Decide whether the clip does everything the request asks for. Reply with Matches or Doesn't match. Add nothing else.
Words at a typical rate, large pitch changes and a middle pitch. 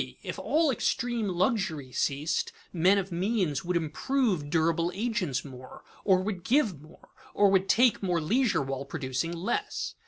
Matches